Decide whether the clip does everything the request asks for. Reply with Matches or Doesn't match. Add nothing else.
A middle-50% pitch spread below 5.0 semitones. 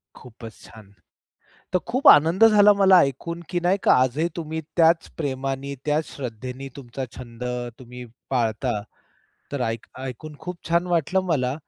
Doesn't match